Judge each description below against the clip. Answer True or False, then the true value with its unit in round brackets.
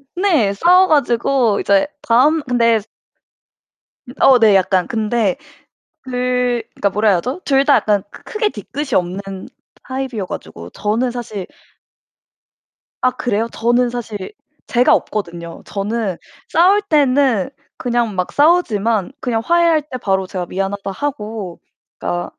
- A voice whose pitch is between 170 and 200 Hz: False (235 Hz)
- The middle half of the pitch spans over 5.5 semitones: False (5.1 semitones)